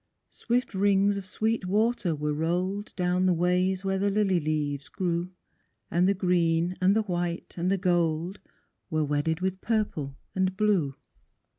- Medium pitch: Yes, medium, 180 Hz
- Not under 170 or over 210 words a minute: No, average, 155 wpm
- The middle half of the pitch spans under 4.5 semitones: Yes, average, 2.8 semitones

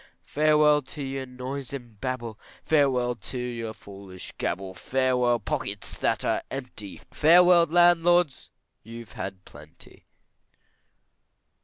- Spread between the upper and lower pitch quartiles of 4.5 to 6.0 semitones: Yes, average, 5.0 semitones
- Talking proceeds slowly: Yes, slow, 110 wpm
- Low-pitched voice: Yes, low, 125 Hz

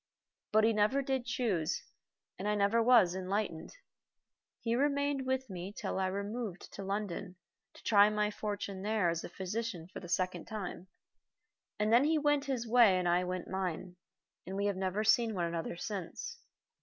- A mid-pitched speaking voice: No, high, 205 Hz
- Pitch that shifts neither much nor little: Yes, average, 3.9 semitones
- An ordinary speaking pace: Yes, average, 175 wpm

